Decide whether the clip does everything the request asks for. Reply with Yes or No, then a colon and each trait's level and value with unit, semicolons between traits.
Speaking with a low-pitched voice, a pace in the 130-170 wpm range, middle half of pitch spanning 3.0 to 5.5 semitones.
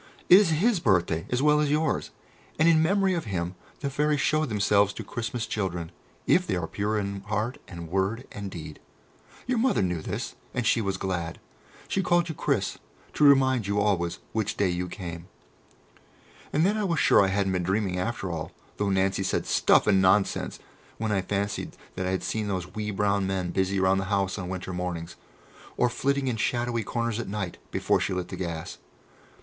No: low, 100 Hz; average, 200 wpm; average, 5.2 semitones